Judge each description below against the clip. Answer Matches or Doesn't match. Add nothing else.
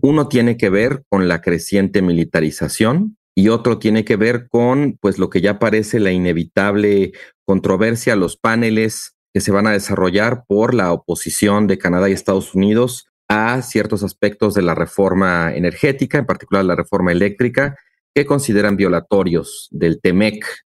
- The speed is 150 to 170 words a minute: Matches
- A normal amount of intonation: Matches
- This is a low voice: Matches